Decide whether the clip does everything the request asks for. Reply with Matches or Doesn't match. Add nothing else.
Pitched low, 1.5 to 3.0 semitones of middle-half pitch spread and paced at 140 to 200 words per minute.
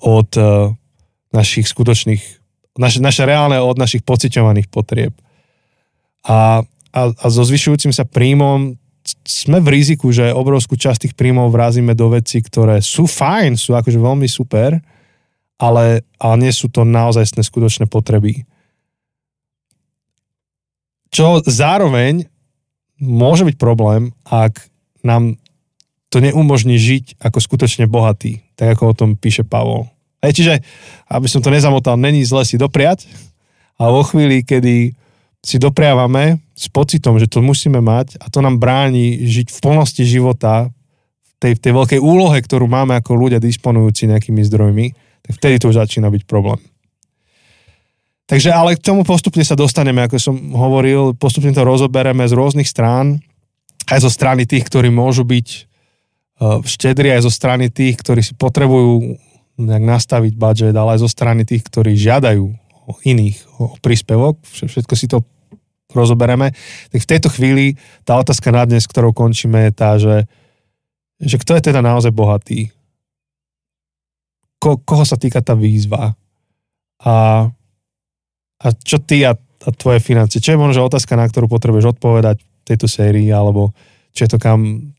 Doesn't match